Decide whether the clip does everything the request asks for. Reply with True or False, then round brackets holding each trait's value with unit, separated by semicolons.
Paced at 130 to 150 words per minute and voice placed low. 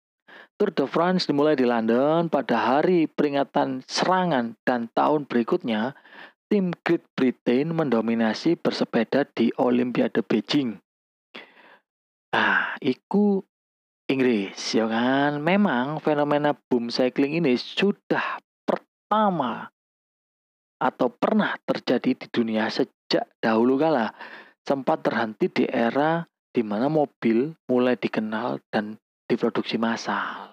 False (105 wpm; 130 Hz)